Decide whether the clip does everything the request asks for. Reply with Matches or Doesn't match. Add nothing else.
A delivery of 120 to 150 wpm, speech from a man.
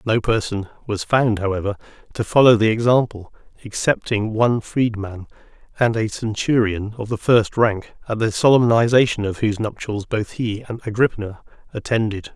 Matches